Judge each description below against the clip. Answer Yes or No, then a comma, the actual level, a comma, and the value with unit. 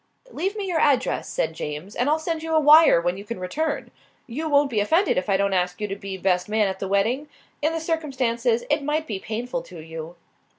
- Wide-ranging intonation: Yes, wide, 8.1 semitones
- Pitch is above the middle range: Yes, high, 240 Hz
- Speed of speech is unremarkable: No, fast, 230 wpm